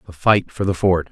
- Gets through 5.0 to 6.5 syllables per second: Yes, 5.3 syllables/s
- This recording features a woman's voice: No, male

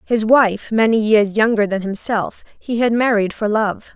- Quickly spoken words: No, average, 180 wpm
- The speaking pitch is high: Yes, high, 215 Hz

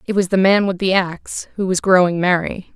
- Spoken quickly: Yes, fast, 240 wpm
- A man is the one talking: No, female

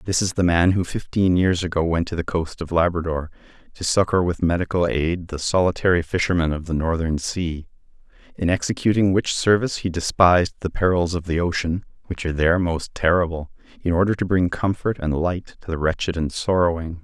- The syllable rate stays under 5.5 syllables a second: No, 5.6 syllables/s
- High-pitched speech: No, very low, 85 Hz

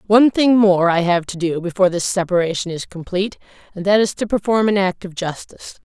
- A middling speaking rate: No, fast, 215 wpm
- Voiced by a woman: Yes, female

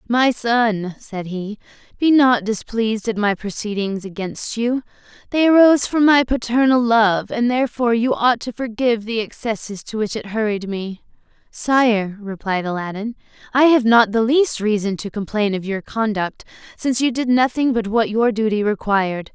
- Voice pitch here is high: Yes, high, 225 Hz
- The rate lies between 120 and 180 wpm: Yes, average, 170 wpm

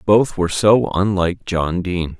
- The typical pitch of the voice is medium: No, very low, 95 Hz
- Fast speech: No, average, 165 wpm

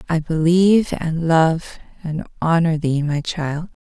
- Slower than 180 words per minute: Yes, average, 140 wpm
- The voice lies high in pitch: No, medium, 160 Hz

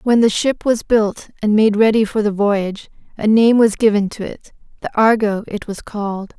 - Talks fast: No, average, 195 wpm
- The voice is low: No, high, 215 Hz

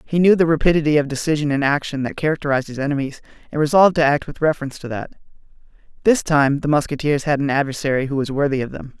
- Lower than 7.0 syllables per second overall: No, 7.1 syllables/s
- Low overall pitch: No, medium, 145 Hz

